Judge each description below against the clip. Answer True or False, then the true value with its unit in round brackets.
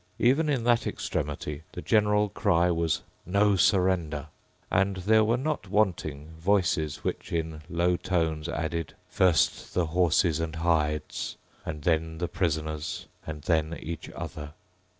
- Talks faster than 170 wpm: False (135 wpm)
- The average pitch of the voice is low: True (85 Hz)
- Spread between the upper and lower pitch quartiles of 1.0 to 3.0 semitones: False (3.7 semitones)